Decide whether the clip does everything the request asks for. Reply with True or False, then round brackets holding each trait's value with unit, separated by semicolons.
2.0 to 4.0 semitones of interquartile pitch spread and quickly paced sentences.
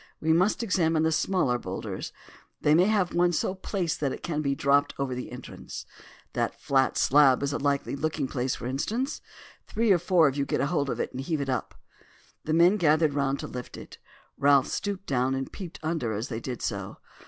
False (4.4 semitones; 210 wpm)